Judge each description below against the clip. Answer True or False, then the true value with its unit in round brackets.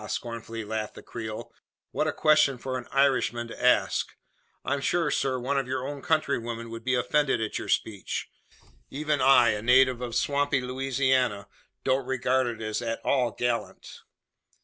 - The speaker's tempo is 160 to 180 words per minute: True (165 wpm)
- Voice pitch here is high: False (125 Hz)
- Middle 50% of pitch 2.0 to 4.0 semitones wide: True (2.7 semitones)